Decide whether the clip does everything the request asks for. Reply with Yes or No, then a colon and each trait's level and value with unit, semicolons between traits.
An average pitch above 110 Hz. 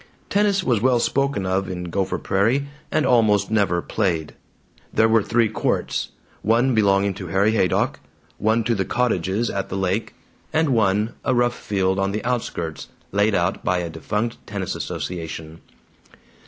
No: low, 105 Hz